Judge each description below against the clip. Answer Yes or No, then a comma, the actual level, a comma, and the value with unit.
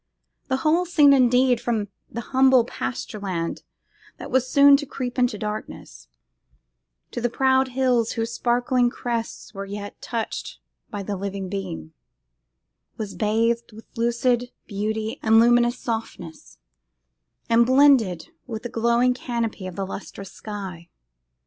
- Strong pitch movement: No, average, 3.3 semitones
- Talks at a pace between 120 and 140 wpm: Yes, slow, 135 wpm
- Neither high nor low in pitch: No, high, 235 Hz